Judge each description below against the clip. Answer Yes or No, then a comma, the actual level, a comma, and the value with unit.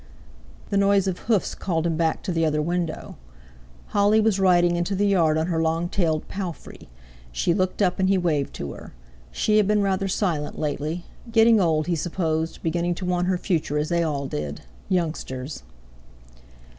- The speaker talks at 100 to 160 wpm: No, average, 175 wpm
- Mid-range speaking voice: Yes, medium, 175 Hz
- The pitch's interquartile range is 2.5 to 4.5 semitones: Yes, average, 3.4 semitones